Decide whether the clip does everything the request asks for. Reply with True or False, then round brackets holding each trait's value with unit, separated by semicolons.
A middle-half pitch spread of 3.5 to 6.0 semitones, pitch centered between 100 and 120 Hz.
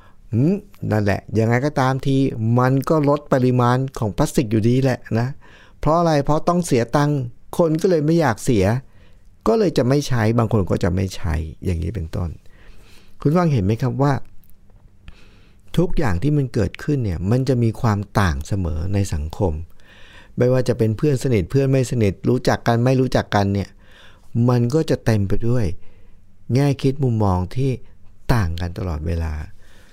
True (5.5 semitones; 110 Hz)